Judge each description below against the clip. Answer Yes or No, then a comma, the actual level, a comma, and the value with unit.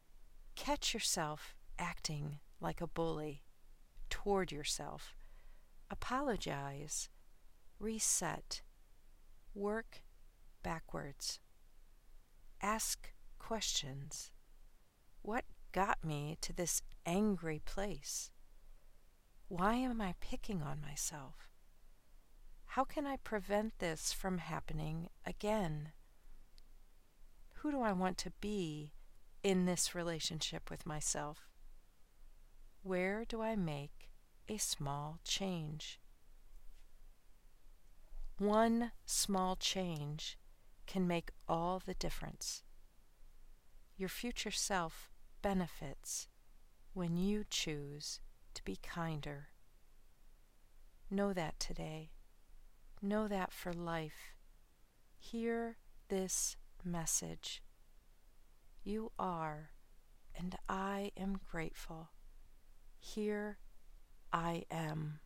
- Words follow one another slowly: Yes, slow, 85 wpm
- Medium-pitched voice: Yes, medium, 165 Hz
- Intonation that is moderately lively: No, wide, 5.9 semitones